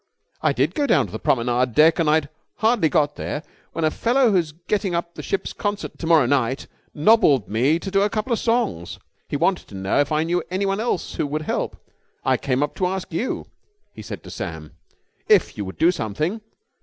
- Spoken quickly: Yes, fast, 215 wpm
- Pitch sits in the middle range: Yes, medium, 160 Hz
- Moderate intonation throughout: No, wide, 6.6 semitones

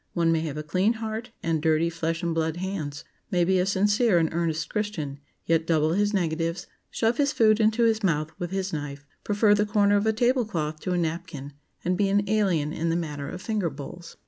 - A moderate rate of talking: No, fast, 220 wpm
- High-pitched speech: No, medium, 175 Hz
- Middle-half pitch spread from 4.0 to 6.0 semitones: Yes, average, 4.5 semitones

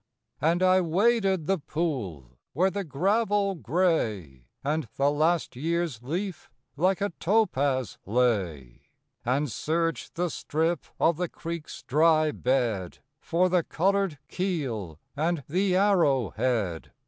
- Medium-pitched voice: Yes, medium, 160 Hz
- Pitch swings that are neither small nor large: No, wide, 6.3 semitones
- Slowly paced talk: Yes, slow, 125 wpm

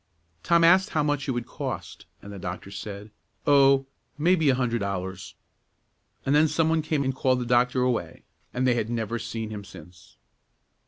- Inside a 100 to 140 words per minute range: No, average, 180 wpm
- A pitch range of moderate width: No, wide, 5.8 semitones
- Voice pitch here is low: Yes, low, 125 Hz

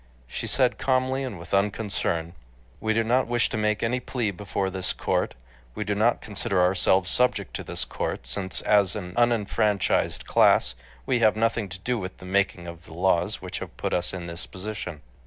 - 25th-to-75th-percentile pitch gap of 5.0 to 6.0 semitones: No, average, 3.8 semitones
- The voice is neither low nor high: No, low, 100 Hz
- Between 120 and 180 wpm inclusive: No, average, 195 wpm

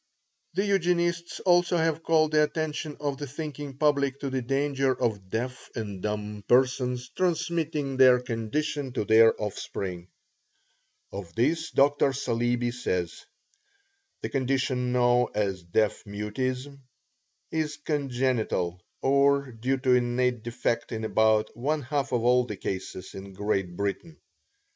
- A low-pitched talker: Yes, low, 130 Hz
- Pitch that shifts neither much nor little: Yes, average, 4.7 semitones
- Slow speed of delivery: Yes, slow, 130 wpm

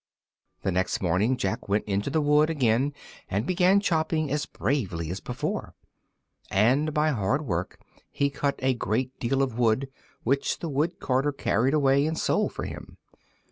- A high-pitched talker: No, low, 135 Hz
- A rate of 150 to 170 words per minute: Yes, average, 165 wpm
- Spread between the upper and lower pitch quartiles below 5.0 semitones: No, wide, 5.4 semitones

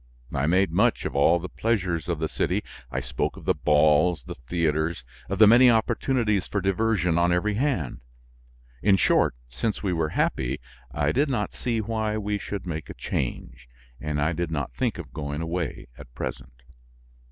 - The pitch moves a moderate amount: No, wide, 5.9 semitones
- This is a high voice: No, very low, 85 Hz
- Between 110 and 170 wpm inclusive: No, average, 180 wpm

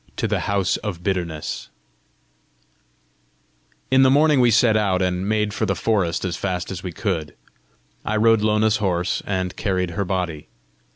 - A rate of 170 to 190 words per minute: No, average, 160 wpm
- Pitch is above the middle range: No, very low, 95 Hz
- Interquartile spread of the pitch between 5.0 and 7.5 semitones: No, average, 3.1 semitones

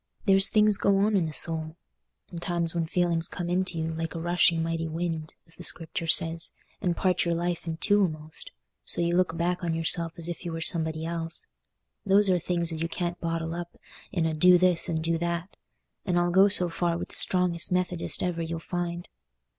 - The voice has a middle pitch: Yes, medium, 170 Hz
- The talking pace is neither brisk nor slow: No, fast, 210 wpm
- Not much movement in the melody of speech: Yes, narrow, 1.5 semitones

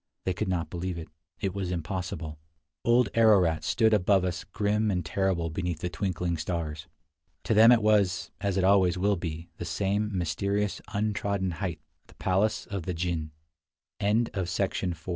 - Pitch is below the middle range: Yes, very low, 95 Hz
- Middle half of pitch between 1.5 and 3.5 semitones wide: Yes, average, 2.9 semitones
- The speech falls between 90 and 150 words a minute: Yes, average, 145 wpm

